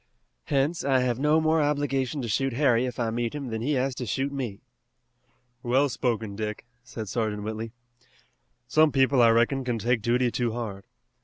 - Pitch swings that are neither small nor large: Yes, average, 3.2 semitones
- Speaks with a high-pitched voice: No, low, 125 Hz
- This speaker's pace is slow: No, average, 180 wpm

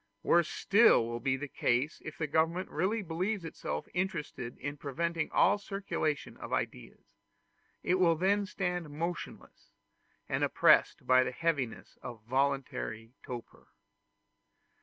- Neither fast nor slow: No, slow, 130 wpm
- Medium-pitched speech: Yes, medium, 160 Hz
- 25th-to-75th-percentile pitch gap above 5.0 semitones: Yes, wide, 5.4 semitones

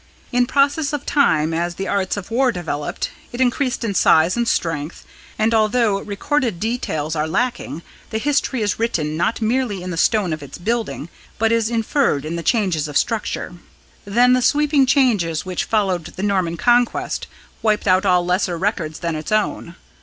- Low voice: No, high, 205 Hz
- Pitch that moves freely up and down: Yes, wide, 6.0 semitones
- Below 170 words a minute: No, average, 175 wpm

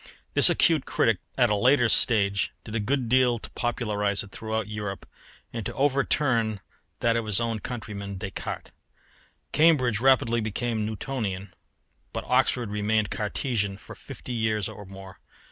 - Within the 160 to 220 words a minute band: No, average, 145 wpm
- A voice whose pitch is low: Yes, low, 110 Hz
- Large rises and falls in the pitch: No, average, 3.0 semitones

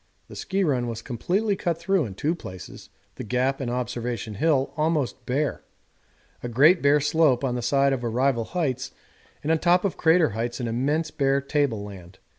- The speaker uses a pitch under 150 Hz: Yes, low, 135 Hz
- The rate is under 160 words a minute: No, average, 185 wpm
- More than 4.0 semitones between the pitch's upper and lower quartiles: Yes, average, 4.9 semitones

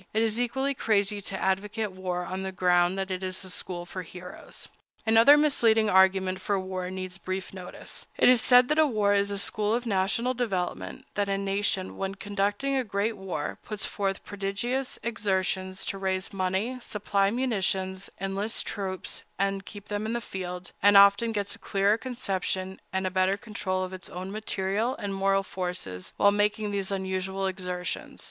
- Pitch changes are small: Yes, narrow, 2.2 semitones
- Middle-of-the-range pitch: No, high, 195 Hz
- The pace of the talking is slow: No, average, 170 wpm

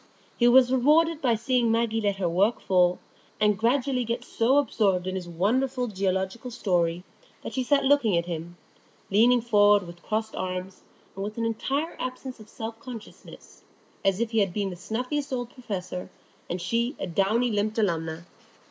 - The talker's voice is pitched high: Yes, high, 220 Hz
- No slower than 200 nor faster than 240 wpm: No, average, 175 wpm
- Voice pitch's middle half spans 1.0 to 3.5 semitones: No, average, 4.8 semitones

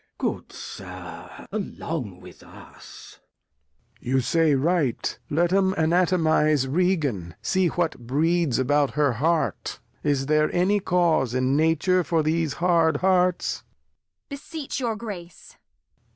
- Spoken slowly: Yes, slow, 110 wpm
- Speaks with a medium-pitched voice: Yes, medium, 160 Hz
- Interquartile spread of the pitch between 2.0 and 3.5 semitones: No, average, 4.1 semitones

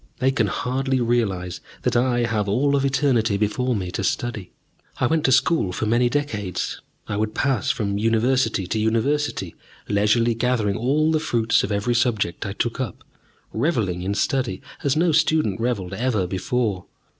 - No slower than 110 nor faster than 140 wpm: No, average, 165 wpm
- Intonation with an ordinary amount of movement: Yes, average, 4.3 semitones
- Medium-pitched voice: No, low, 115 Hz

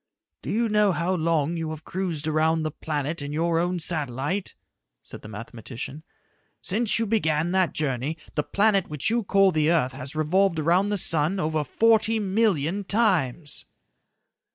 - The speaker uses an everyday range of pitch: Yes, average, 4.6 semitones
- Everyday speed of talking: Yes, average, 160 wpm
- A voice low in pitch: No, medium, 165 Hz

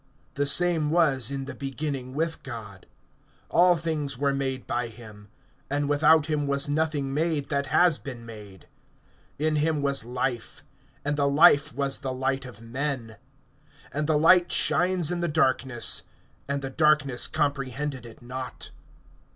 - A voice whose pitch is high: No, medium, 140 Hz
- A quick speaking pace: No, average, 150 wpm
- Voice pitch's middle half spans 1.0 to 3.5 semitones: Yes, average, 2.9 semitones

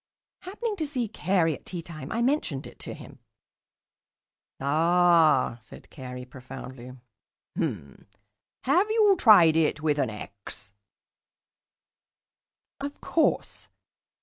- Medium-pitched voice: Yes, medium, 165 Hz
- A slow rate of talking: Yes, slow, 105 wpm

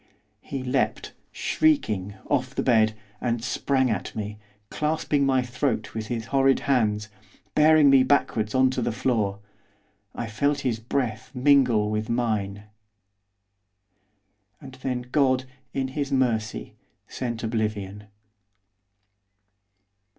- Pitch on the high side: No, low, 125 Hz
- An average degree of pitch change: Yes, average, 3.7 semitones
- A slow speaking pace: Yes, slow, 115 wpm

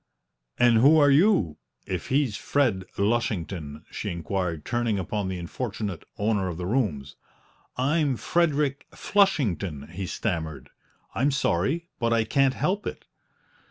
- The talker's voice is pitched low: Yes, low, 110 Hz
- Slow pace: Yes, slow, 130 wpm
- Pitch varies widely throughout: Yes, wide, 7.6 semitones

